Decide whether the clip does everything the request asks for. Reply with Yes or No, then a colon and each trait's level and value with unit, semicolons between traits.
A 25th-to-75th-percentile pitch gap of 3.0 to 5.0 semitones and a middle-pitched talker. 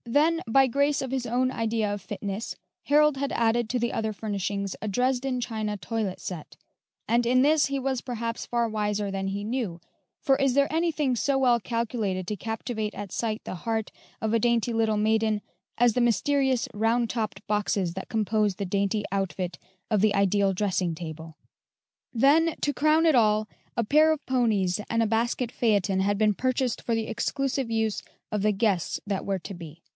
No: average, 3.6 semitones; high, 225 Hz